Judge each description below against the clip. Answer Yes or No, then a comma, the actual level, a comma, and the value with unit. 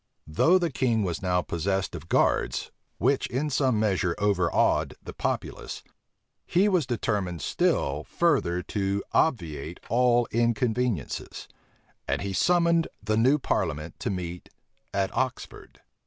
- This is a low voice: Yes, low, 105 Hz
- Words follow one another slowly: Yes, slow, 125 wpm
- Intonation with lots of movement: Yes, wide, 6.4 semitones